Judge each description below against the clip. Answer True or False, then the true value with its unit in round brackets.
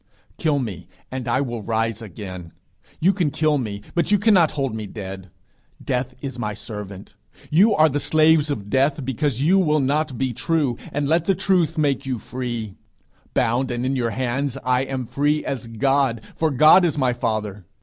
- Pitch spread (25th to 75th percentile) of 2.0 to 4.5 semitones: False (5.0 semitones)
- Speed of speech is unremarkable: True (185 wpm)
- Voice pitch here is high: False (130 Hz)